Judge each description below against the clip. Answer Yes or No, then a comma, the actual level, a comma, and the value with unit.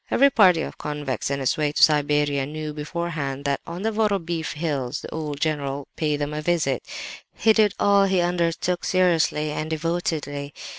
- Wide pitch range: No, average, 3.2 semitones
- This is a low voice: No, medium, 155 Hz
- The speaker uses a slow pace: No, average, 180 wpm